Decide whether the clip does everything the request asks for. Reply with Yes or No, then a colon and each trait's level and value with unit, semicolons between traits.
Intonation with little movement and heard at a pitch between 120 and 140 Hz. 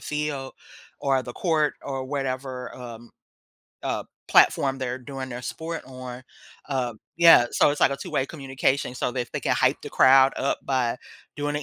Yes: narrow, 2.0 semitones; low, 135 Hz